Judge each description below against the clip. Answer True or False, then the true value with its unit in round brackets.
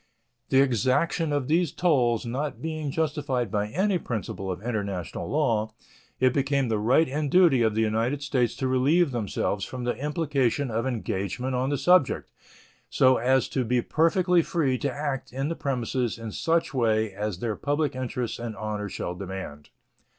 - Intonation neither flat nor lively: True (4.6 semitones)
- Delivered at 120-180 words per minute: True (170 wpm)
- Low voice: True (130 Hz)